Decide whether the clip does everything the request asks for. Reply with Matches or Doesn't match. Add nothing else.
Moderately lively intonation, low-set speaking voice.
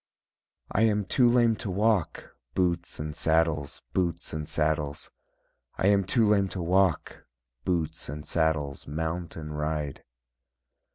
Matches